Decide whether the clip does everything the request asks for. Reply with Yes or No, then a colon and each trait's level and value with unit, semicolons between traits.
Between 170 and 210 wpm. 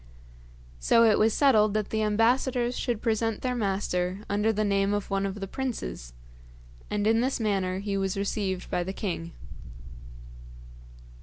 No: average, 155 wpm